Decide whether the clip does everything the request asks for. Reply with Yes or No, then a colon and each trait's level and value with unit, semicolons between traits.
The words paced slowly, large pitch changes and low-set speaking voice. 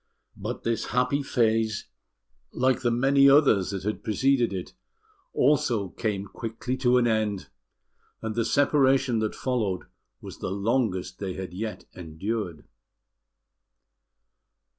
No: slow, 120 wpm; average, 4.4 semitones; low, 115 Hz